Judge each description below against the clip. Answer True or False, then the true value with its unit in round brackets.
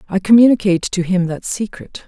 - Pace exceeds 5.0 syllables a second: True (5.9 syllables/s)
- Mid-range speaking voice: False (195 Hz)